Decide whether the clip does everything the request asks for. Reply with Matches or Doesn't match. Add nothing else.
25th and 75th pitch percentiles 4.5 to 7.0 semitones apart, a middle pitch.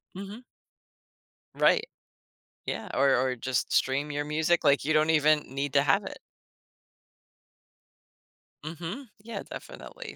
Doesn't match